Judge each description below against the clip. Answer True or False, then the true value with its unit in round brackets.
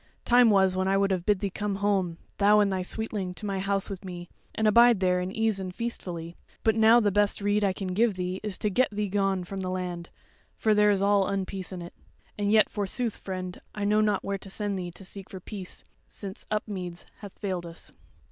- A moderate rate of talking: False (230 wpm)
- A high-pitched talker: True (195 Hz)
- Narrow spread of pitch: True (2.1 semitones)